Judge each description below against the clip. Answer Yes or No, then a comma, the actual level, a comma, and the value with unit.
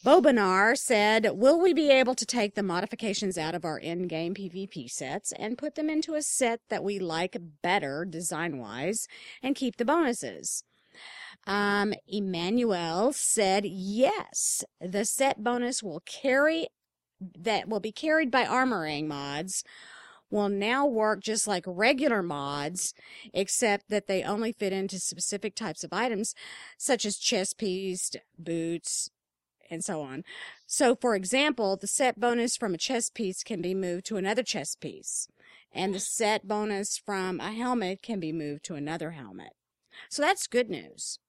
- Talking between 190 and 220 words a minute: No, average, 155 wpm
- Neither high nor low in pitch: No, high, 205 Hz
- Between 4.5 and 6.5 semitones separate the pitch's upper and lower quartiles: Yes, average, 5.1 semitones